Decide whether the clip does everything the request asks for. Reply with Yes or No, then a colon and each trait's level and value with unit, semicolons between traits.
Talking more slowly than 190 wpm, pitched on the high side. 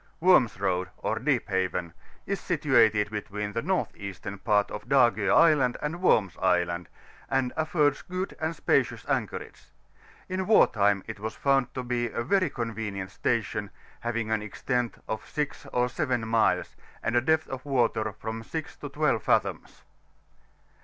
No: average, 155 wpm; low, 115 Hz